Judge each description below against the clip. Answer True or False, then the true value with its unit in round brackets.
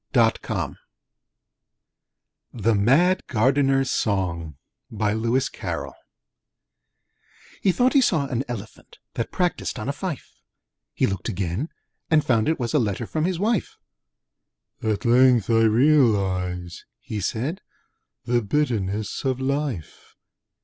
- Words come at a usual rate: False (115 wpm)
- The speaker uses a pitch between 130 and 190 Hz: False (120 Hz)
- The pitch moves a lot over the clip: True (5.7 semitones)